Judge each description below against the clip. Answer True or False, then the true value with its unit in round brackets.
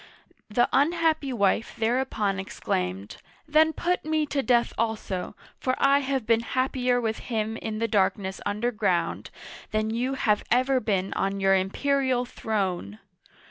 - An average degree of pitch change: True (4.7 semitones)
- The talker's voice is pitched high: True (230 Hz)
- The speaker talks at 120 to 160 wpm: True (140 wpm)